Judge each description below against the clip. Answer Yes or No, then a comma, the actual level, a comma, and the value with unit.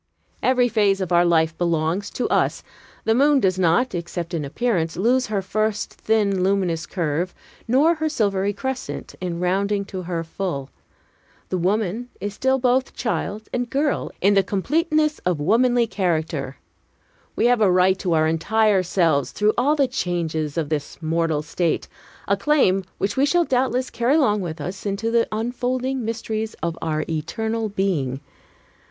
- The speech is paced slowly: No, average, 160 wpm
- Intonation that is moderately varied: No, wide, 5.9 semitones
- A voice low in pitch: No, high, 200 Hz